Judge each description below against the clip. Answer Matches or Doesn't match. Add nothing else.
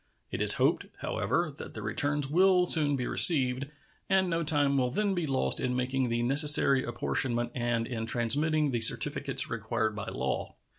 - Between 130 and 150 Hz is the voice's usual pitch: Matches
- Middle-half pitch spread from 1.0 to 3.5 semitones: Doesn't match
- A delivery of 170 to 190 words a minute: Matches